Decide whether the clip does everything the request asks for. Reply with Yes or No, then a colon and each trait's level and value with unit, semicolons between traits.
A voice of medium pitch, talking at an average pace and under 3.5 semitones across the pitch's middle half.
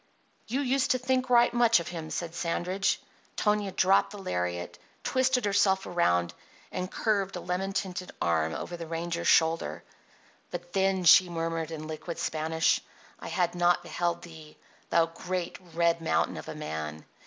Yes: medium, 175 Hz; average, 160 wpm; average, 3.0 semitones